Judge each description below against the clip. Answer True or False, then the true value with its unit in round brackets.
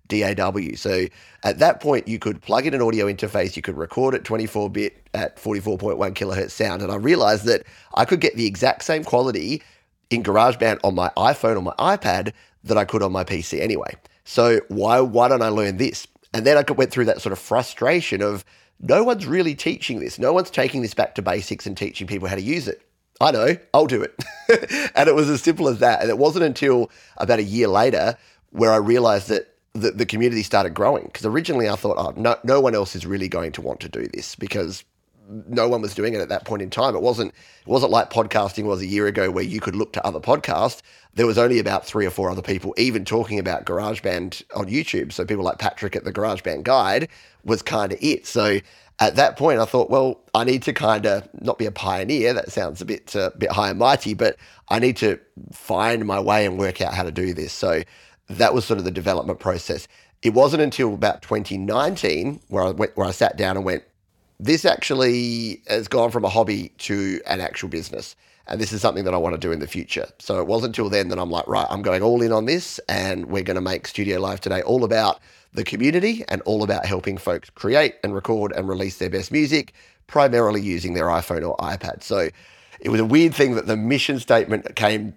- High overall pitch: False (110 Hz)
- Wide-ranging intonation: False (3.8 semitones)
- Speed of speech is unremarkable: False (230 wpm)